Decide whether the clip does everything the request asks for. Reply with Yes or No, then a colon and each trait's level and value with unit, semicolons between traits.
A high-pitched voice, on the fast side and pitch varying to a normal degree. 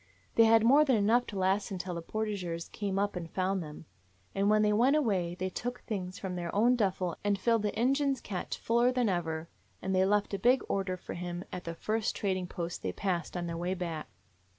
Yes: high, 195 Hz; fast, 220 wpm; average, 3.8 semitones